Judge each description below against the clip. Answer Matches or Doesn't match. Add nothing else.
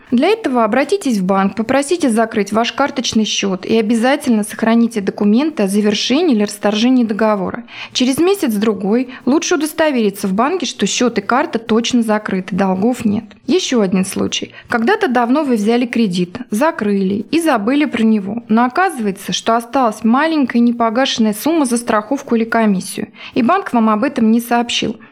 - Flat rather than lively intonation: Doesn't match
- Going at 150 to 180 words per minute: Matches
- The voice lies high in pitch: Matches